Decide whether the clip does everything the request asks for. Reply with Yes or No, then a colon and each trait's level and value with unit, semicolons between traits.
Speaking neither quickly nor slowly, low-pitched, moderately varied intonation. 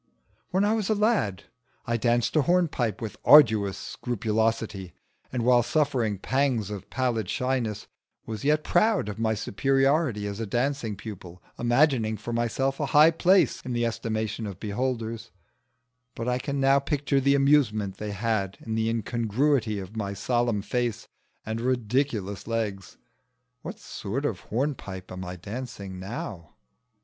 Yes: average, 150 wpm; low, 115 Hz; average, 4.4 semitones